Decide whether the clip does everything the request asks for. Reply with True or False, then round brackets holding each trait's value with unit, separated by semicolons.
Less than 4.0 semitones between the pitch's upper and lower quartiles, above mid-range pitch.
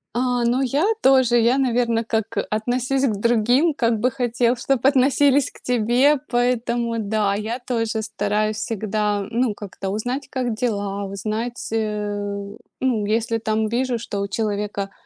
True (2.7 semitones; 230 Hz)